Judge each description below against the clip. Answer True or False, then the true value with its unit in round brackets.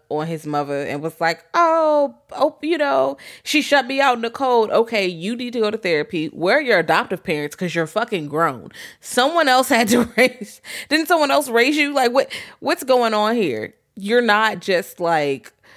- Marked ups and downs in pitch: True (8.3 semitones)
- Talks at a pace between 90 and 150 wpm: False (200 wpm)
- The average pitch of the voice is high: True (225 Hz)